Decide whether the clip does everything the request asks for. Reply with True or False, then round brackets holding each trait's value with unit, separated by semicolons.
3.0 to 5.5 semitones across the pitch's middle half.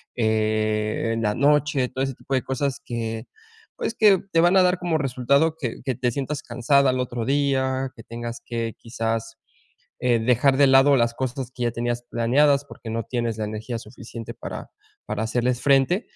True (3.3 semitones)